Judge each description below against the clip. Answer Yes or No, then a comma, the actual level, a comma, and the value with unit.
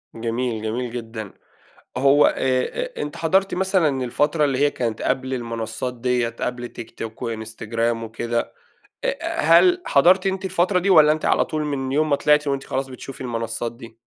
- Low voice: Yes, low, 130 Hz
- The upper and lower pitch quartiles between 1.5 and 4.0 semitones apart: No, average, 4.6 semitones